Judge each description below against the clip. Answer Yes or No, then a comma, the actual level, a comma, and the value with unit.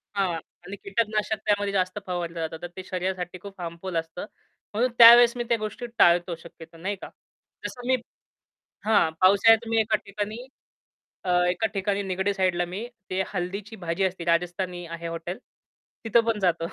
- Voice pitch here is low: No, high, 190 Hz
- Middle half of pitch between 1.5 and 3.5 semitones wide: Yes, average, 3.2 semitones